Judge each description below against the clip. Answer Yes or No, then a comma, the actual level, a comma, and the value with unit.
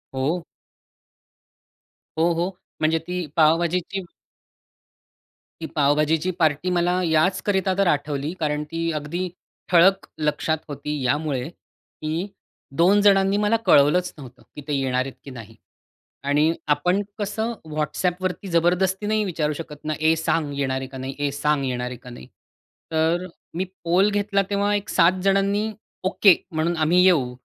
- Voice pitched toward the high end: No, medium, 165 Hz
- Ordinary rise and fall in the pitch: Yes, average, 4.0 semitones